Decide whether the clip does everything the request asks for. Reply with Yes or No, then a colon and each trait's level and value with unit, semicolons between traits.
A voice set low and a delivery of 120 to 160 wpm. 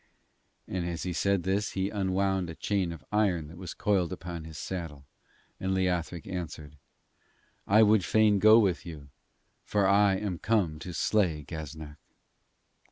Yes: very low, 90 Hz; average, 155 wpm